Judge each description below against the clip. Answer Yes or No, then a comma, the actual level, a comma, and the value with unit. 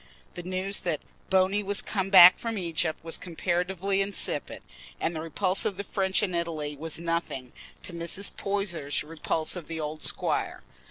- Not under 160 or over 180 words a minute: Yes, average, 165 wpm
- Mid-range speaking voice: Yes, medium, 175 Hz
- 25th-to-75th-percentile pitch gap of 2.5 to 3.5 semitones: Yes, average, 3.0 semitones